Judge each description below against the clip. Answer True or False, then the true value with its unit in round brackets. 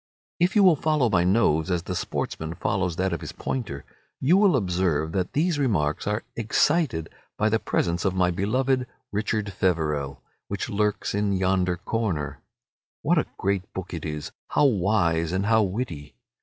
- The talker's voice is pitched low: True (95 Hz)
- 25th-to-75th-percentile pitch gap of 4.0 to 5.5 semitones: True (5.1 semitones)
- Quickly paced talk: False (170 wpm)